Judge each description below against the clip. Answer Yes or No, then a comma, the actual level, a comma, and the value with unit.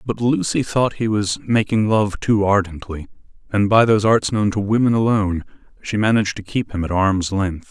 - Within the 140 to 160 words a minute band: No, average, 195 wpm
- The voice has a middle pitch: No, low, 105 Hz